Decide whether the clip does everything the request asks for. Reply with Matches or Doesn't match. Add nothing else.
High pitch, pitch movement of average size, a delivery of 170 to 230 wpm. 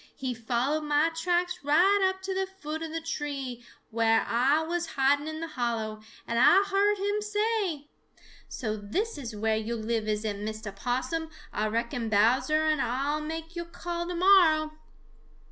Doesn't match